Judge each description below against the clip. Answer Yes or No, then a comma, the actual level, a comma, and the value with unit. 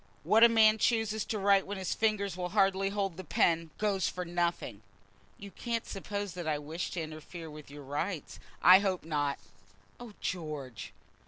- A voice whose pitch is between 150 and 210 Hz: Yes, medium, 185 Hz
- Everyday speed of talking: Yes, average, 175 wpm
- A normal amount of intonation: Yes, average, 4.0 semitones